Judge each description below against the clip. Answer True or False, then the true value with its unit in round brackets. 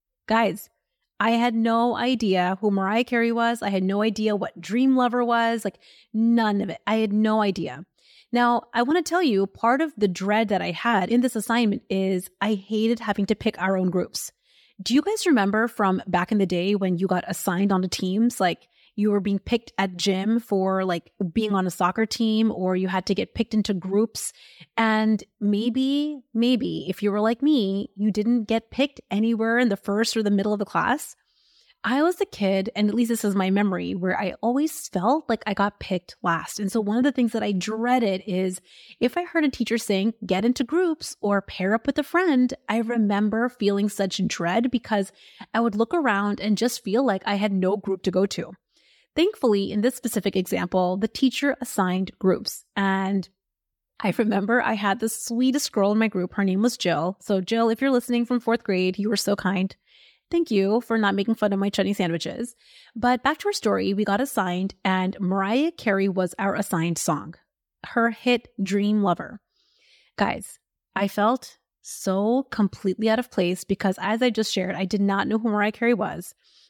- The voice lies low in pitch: False (210 Hz)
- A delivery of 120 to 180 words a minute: False (205 wpm)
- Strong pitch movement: False (3.4 semitones)